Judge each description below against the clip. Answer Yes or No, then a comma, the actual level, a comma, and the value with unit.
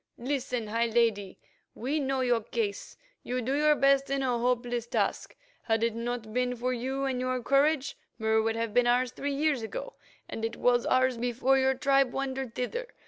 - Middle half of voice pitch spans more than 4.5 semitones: No, narrow, 2.6 semitones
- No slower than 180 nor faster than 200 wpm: Yes, average, 190 wpm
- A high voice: Yes, very high, 250 Hz